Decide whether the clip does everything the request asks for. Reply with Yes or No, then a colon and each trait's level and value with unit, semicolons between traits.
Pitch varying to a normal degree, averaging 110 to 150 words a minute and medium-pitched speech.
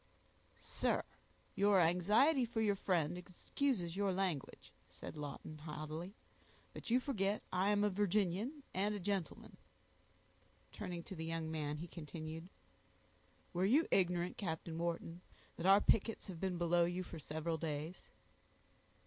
Yes: average, 3.6 semitones; average, 140 wpm; medium, 180 Hz